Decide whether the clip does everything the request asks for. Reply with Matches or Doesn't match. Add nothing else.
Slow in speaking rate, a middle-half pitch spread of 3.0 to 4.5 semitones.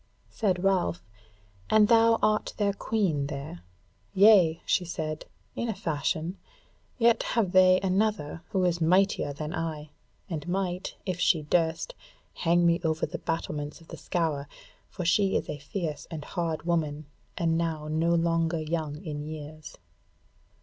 Doesn't match